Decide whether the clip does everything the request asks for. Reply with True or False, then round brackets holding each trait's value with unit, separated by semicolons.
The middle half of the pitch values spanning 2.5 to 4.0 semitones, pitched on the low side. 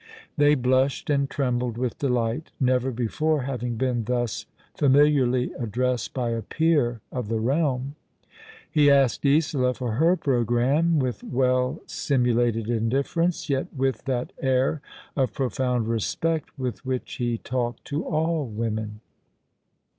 True (2.8 semitones; 130 Hz)